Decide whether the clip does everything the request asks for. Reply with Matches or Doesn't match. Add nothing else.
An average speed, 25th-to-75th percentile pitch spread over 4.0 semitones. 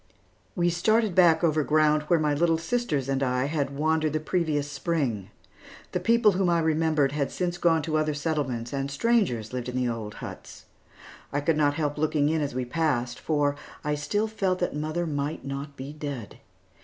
Doesn't match